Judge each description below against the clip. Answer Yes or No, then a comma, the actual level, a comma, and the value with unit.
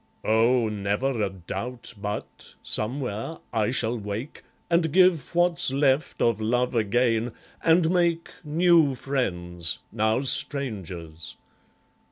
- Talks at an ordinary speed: No, slow, 110 wpm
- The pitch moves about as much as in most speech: No, wide, 5.7 semitones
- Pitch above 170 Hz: No, low, 120 Hz